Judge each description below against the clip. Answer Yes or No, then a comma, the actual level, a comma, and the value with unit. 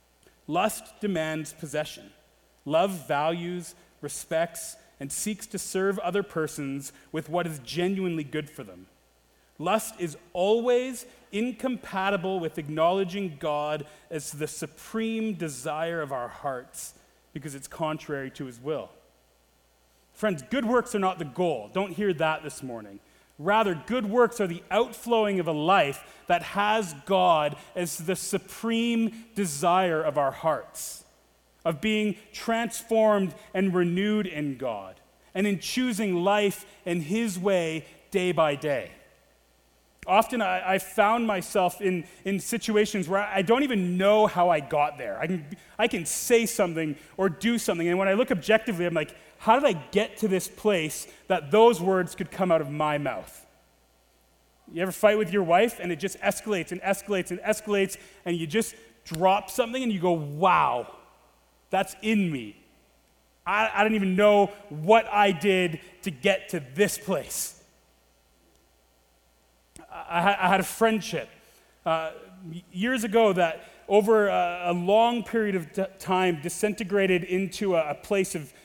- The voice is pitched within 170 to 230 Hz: Yes, medium, 185 Hz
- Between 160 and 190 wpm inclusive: No, average, 150 wpm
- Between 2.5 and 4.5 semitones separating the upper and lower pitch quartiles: No, average, 4.9 semitones